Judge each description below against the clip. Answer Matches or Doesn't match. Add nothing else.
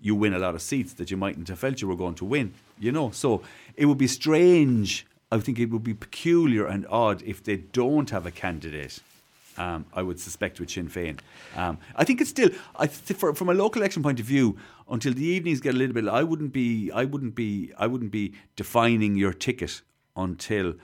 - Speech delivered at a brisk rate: Matches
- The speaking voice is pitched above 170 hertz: Doesn't match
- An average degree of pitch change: Doesn't match